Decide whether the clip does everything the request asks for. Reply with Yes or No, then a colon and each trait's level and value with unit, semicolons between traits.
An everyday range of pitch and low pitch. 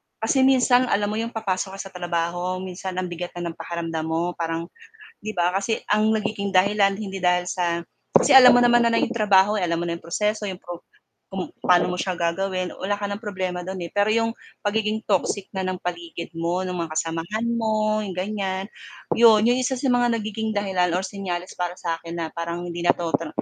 No: average, 3.5 semitones; high, 190 Hz